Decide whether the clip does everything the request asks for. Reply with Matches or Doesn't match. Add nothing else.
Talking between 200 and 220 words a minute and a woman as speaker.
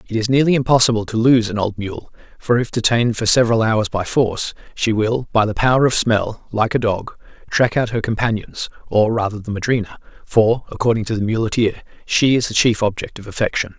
Doesn't match